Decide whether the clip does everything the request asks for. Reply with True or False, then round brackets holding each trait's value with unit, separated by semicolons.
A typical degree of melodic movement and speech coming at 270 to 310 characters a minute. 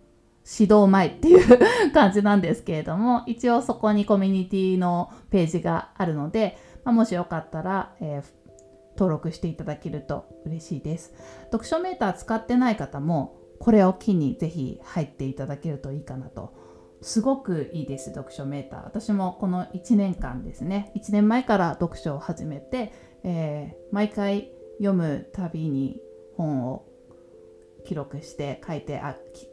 False (6.4 semitones; 300 characters per minute)